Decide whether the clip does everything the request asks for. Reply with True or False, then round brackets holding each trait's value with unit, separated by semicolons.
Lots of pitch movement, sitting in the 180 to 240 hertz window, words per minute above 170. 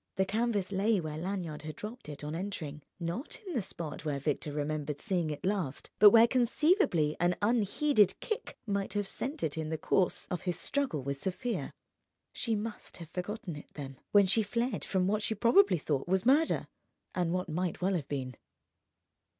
True (5.8 semitones; 185 Hz; 185 wpm)